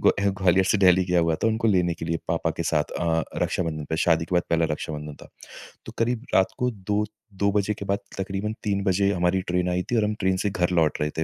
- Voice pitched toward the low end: Yes, very low, 95 Hz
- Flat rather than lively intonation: No, average, 3.5 semitones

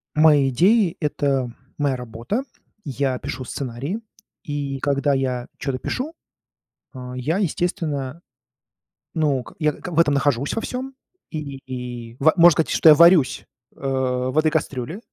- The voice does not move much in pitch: No, average, 3.8 semitones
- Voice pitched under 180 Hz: Yes, medium, 140 Hz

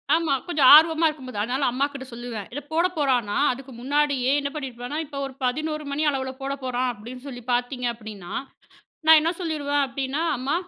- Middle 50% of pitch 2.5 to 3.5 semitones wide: Yes, average, 3.0 semitones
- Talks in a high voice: Yes, very high, 270 Hz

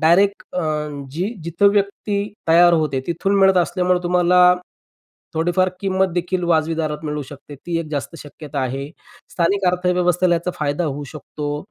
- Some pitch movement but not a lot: Yes, average, 3.0 semitones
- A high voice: No, medium, 175 Hz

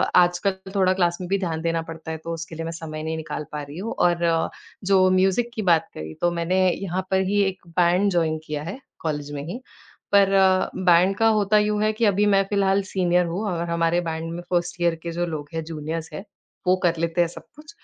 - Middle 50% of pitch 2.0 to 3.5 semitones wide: Yes, average, 2.7 semitones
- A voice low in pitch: No, medium, 175 Hz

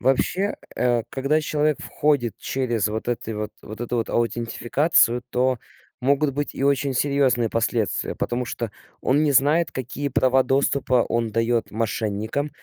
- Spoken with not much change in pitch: No, average, 3.4 semitones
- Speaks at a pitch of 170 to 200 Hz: No, low, 125 Hz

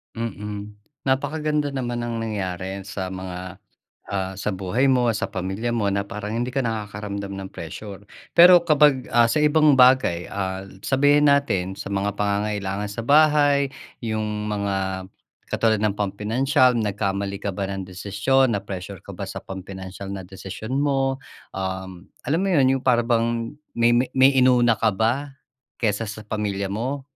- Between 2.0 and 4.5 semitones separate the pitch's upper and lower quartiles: No, average, 4.9 semitones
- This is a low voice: Yes, low, 105 Hz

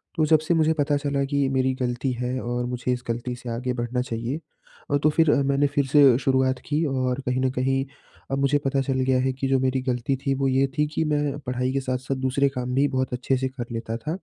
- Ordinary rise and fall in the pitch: No, narrow, 1.9 semitones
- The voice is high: No, low, 130 Hz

